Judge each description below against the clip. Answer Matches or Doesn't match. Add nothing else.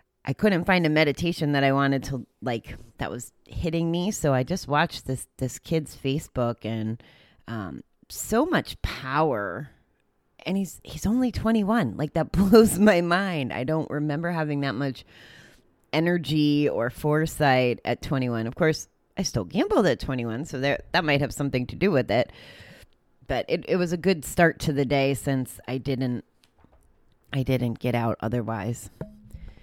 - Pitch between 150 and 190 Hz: Doesn't match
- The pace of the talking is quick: Doesn't match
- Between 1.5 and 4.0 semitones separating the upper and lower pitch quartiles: Doesn't match